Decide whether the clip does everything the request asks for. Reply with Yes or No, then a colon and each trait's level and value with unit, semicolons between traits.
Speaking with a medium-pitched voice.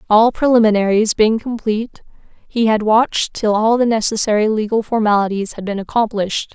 No: high, 220 Hz